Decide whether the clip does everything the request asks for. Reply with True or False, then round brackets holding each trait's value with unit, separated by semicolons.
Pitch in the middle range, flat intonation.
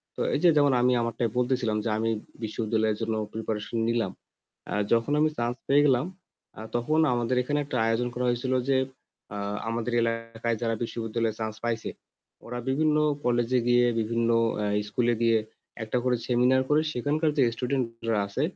False (120 Hz; 2.0 semitones)